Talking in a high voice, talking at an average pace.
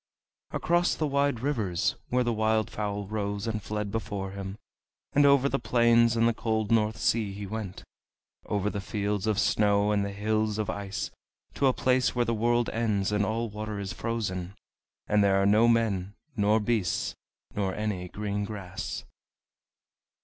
No: low, 105 Hz; average, 170 wpm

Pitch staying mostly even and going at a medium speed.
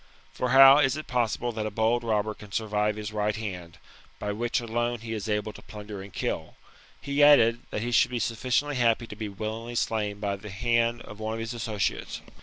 No: narrow, 2.2 semitones; fast, 215 wpm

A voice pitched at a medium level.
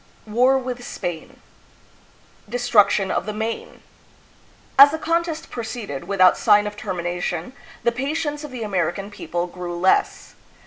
No: high, 215 Hz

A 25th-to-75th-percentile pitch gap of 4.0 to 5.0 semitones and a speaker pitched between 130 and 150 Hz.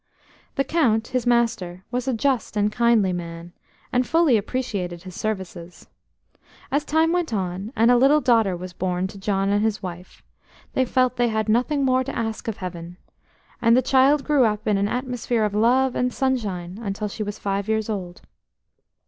No: average, 4.7 semitones; high, 220 Hz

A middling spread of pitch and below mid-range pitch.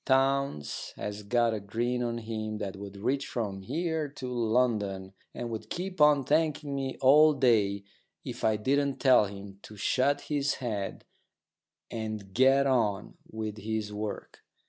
Yes: average, 4.7 semitones; low, 115 Hz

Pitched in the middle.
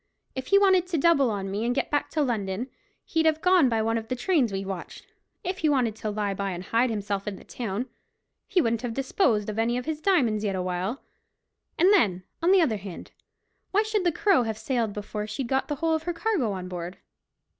No: high, 240 Hz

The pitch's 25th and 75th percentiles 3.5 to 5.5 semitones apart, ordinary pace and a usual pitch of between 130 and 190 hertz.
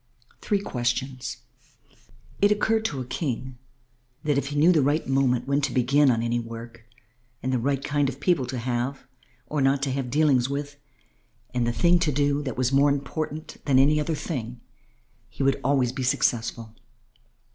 No: average, 2.8 semitones; average, 180 wpm; low, 135 Hz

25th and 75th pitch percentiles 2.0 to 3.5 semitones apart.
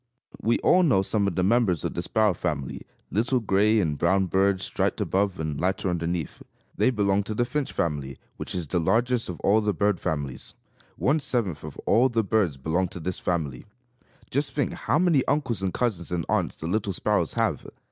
No: average, 5.0 semitones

